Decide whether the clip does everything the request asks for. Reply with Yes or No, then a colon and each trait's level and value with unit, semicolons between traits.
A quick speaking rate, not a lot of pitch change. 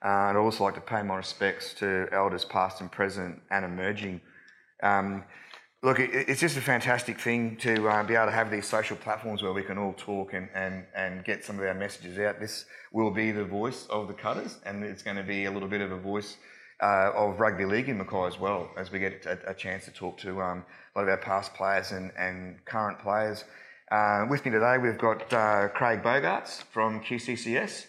Yes: fast, 225 wpm; narrow, 2.2 semitones